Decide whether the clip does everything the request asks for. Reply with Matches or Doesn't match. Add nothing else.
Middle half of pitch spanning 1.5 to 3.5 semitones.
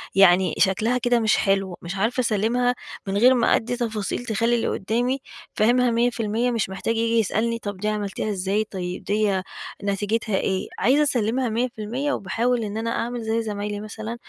Matches